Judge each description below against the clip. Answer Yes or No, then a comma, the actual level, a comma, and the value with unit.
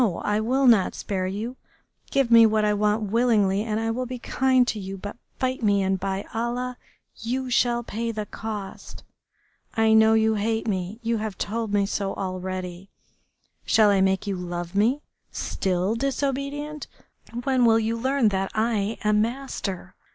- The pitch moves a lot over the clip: No, average, 3.3 semitones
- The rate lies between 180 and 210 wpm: No, average, 165 wpm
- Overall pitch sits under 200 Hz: No, high, 220 Hz